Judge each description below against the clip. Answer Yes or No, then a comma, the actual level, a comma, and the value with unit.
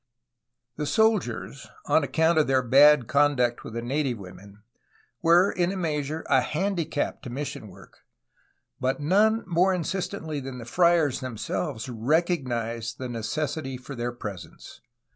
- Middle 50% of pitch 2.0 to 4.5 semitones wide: No, average, 5.3 semitones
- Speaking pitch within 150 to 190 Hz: No, medium, 140 Hz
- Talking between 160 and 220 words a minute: No, average, 145 wpm